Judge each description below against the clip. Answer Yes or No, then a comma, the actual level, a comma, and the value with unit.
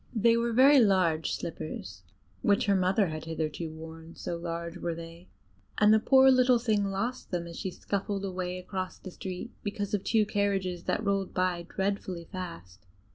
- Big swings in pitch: No, average, 3.5 semitones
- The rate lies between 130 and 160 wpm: No, average, 175 wpm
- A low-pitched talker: No, medium, 185 Hz